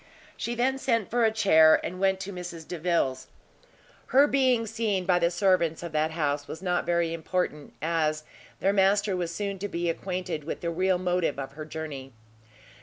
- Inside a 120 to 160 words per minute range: No, average, 180 wpm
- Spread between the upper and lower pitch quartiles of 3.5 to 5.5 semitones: Yes, average, 3.8 semitones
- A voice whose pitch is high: No, medium, 180 Hz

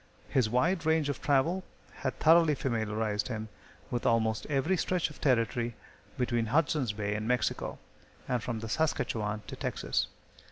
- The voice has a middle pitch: No, low, 125 Hz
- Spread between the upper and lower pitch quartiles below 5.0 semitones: No, average, 5.3 semitones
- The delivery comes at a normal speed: Yes, average, 150 wpm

